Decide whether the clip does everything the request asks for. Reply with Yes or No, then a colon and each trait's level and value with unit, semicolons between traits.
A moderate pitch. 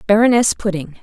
No: high, 205 Hz